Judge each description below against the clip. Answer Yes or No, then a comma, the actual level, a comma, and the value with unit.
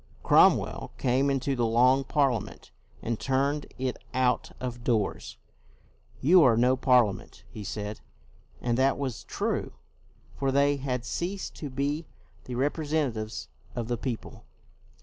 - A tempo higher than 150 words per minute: No, slow, 135 wpm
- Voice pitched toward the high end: No, low, 130 Hz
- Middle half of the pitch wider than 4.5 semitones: No, average, 2.8 semitones